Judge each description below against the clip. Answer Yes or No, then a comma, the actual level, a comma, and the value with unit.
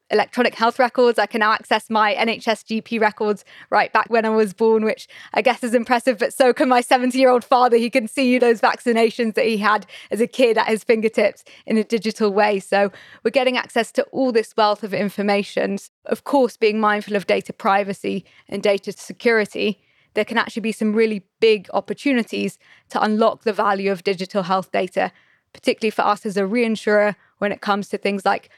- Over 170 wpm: Yes, fast, 205 wpm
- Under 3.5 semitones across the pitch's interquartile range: Yes, narrow, 2.5 semitones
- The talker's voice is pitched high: Yes, high, 220 Hz